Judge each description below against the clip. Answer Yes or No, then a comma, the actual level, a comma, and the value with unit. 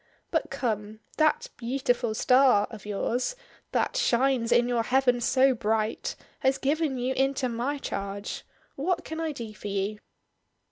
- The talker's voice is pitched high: Yes, high, 245 Hz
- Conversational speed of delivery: Yes, average, 145 wpm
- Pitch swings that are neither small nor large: Yes, average, 3.8 semitones